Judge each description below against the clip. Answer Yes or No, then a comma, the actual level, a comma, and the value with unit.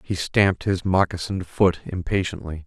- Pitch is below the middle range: Yes, very low, 90 Hz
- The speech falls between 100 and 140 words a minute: Yes, slow, 135 wpm